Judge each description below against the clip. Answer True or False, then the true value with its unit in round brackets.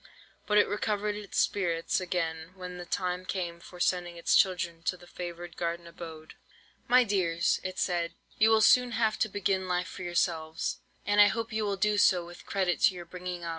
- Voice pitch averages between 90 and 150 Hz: False (180 Hz)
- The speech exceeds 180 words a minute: True (200 wpm)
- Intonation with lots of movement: False (3.0 semitones)